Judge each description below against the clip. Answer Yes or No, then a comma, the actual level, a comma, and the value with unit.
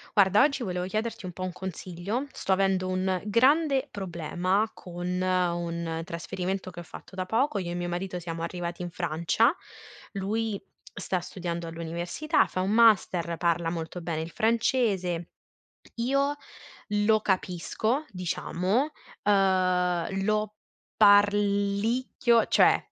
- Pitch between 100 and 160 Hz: No, medium, 185 Hz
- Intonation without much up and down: No, average, 3.5 semitones